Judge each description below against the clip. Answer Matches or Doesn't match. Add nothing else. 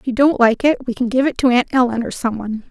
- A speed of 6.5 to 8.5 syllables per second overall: Matches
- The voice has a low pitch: Doesn't match